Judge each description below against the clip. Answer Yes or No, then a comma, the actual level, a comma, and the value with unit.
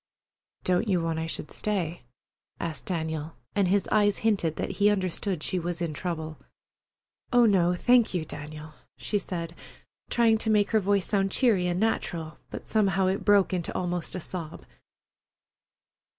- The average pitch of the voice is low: No, medium, 185 Hz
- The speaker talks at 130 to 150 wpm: No, average, 160 wpm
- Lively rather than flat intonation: No, average, 3.7 semitones